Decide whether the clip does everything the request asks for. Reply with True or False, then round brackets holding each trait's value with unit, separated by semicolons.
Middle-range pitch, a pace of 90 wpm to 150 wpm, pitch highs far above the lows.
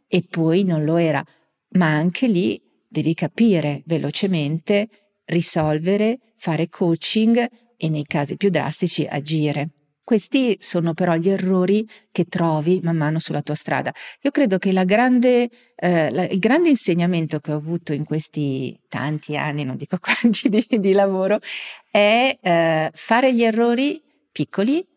True (180 Hz; 145 wpm; 5.7 semitones)